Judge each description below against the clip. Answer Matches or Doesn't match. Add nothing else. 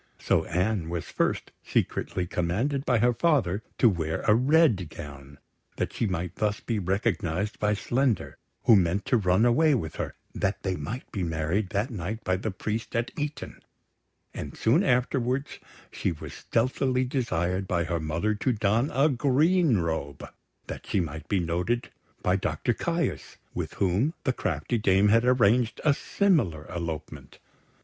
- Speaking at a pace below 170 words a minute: Matches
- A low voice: Matches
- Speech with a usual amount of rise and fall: Doesn't match